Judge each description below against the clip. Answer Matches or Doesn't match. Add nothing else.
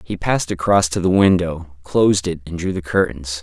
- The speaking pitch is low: Matches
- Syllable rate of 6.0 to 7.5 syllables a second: Doesn't match